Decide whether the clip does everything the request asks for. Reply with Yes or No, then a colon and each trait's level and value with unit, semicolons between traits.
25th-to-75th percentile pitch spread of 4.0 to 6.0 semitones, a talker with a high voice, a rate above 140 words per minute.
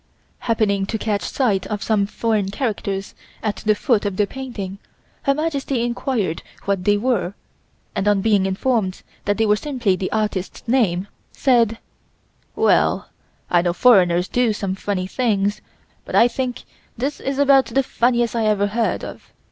No: average, 3.6 semitones; high, 215 Hz; average, 155 wpm